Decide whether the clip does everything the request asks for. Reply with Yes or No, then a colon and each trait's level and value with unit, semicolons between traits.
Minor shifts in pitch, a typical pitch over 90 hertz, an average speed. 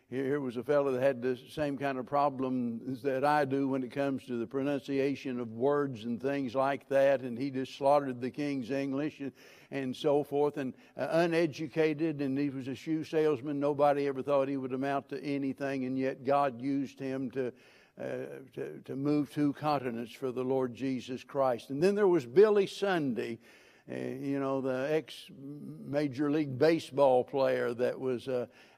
Yes: narrow, 1.9 semitones; low, 135 Hz; average, 185 wpm